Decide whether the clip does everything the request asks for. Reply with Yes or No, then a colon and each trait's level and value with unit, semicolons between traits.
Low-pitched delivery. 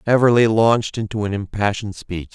Yes: low, 105 Hz